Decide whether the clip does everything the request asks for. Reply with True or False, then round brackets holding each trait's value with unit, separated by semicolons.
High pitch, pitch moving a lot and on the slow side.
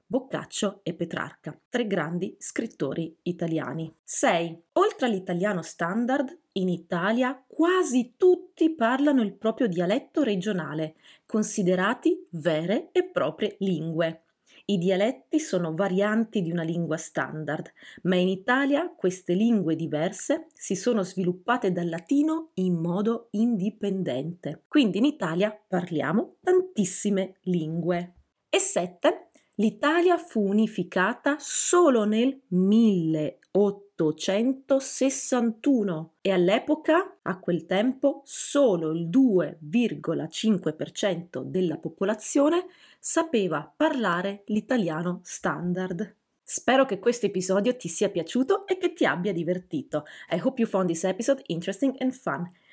True (205 Hz; 6.8 semitones; 110 wpm)